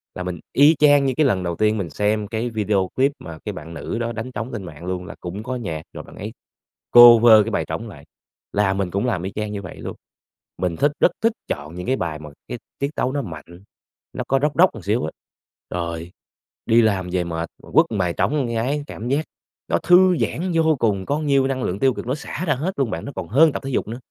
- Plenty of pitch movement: Yes, wide, 6.8 semitones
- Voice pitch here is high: No, low, 110 Hz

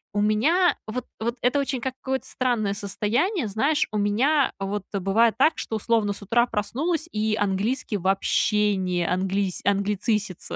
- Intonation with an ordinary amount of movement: Yes, average, 4.1 semitones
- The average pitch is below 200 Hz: No, high, 215 Hz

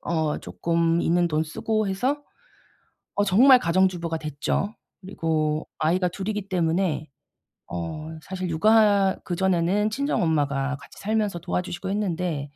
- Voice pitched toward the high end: No, medium, 180 Hz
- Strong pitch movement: No, average, 3.9 semitones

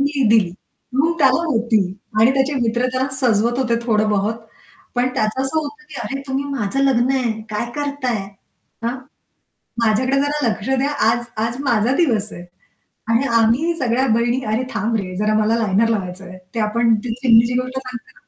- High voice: Yes, high, 240 Hz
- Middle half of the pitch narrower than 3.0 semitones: No, average, 3.3 semitones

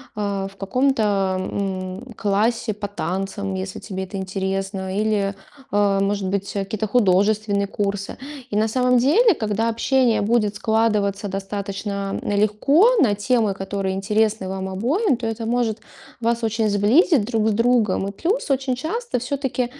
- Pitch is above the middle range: Yes, high, 210 Hz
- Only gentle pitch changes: No, average, 3.2 semitones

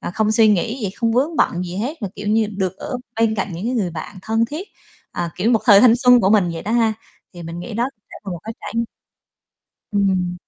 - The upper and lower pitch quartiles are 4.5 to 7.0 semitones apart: No, average, 3.8 semitones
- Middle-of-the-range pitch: No, high, 215 Hz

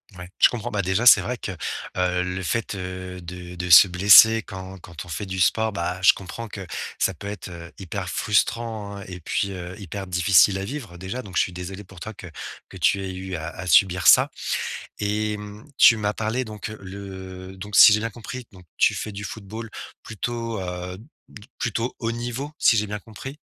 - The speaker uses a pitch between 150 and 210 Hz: No, low, 100 Hz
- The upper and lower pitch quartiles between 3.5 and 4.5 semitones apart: No, average, 3.0 semitones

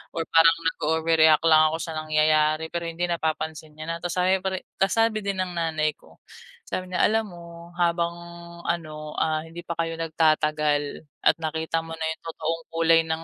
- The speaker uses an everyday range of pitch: No, narrow, 1.5 semitones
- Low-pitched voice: No, medium, 165 Hz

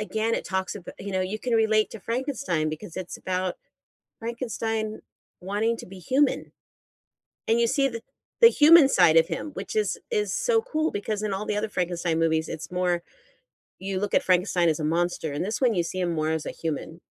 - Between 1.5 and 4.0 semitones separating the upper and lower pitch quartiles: No, average, 4.8 semitones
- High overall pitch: Yes, high, 200 Hz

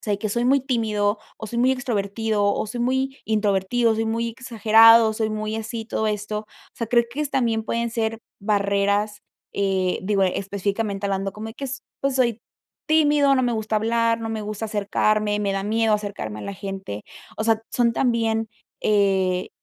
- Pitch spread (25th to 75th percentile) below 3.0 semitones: Yes, narrow, 2.4 semitones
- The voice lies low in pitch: No, high, 220 Hz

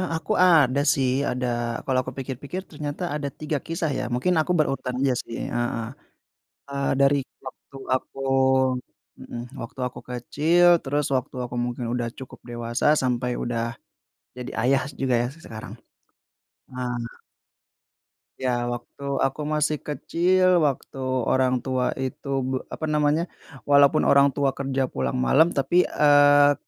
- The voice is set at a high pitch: No, low, 135 Hz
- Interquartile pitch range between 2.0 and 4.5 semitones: Yes, average, 2.9 semitones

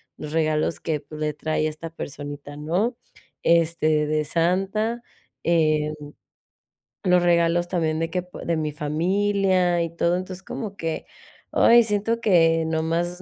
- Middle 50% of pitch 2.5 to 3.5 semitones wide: Yes, average, 2.9 semitones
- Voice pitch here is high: No, medium, 165 Hz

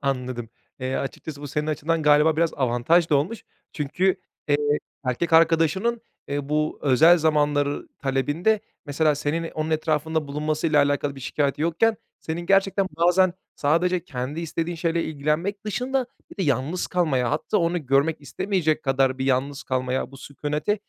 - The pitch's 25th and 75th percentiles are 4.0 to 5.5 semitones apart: No, average, 3.1 semitones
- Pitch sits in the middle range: Yes, medium, 155 Hz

